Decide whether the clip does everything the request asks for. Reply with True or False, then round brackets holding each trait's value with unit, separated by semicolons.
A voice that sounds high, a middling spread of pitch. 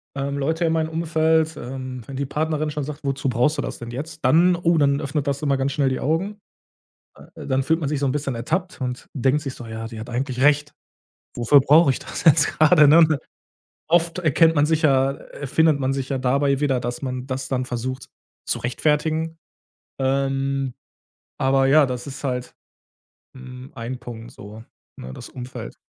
False (140 Hz; 3.1 semitones)